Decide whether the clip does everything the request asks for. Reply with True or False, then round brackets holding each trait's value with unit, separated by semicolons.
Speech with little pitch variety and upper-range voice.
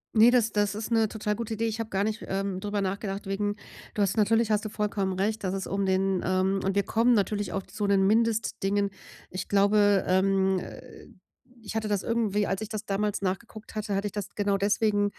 True (1.8 semitones; 205 Hz)